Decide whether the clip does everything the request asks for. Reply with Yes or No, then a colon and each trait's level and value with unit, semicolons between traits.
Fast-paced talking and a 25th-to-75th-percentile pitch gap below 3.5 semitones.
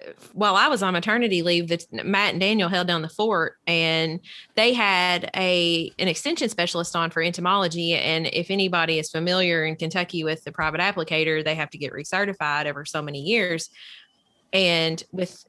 No: average, 175 wpm; average, 2.9 semitones